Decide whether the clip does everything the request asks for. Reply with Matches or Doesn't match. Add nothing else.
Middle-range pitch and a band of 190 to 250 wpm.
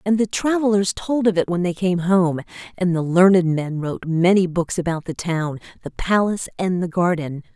Matches